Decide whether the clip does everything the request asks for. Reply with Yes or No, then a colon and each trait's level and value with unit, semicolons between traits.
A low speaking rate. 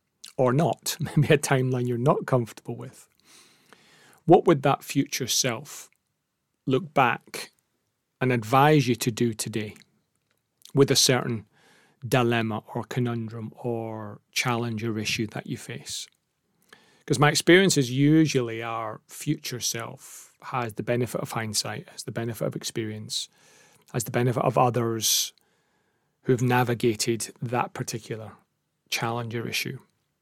Yes: slow, 130 wpm